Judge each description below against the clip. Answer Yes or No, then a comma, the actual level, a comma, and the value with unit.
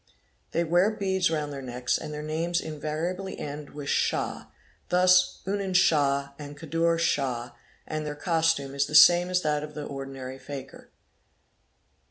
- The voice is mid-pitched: Yes, medium, 155 Hz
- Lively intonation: No, average, 3.7 semitones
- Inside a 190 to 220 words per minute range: No, average, 155 wpm